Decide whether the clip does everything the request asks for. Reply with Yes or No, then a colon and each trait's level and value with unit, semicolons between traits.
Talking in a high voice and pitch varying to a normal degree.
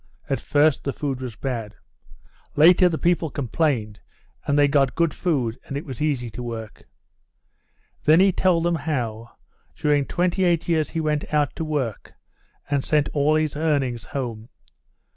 No: medium, 145 Hz; average, 4.2 semitones